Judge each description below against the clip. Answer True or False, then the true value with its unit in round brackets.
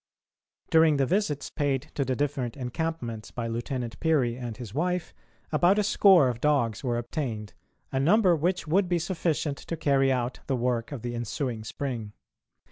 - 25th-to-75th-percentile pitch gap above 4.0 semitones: True (5.1 semitones)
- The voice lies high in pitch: False (135 Hz)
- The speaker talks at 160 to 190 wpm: True (170 wpm)